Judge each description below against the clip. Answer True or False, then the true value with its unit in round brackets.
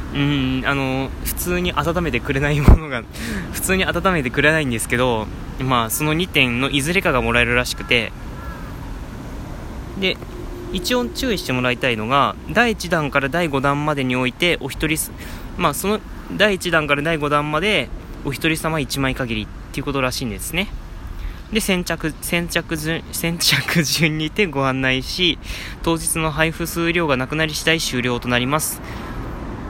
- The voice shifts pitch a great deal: False (4.7 semitones)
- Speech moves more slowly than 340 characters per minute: True (305 characters per minute)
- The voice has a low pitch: False (145 Hz)